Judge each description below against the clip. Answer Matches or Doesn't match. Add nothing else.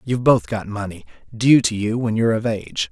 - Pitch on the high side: Doesn't match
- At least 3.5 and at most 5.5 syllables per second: Doesn't match